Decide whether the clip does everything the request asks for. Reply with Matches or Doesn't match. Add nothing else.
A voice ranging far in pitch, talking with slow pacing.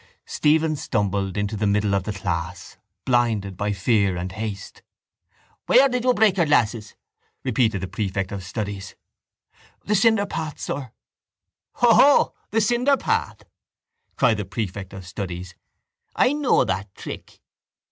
Matches